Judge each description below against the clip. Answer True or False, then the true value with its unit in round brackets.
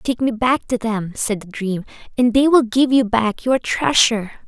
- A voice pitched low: False (230 Hz)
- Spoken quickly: True (215 wpm)